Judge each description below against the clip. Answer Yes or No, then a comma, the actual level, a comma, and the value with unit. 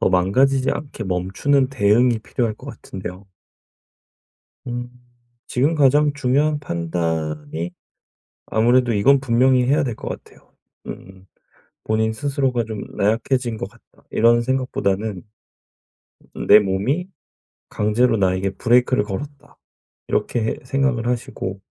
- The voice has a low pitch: Yes, low, 115 Hz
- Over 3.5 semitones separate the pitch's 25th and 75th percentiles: Yes, average, 5.1 semitones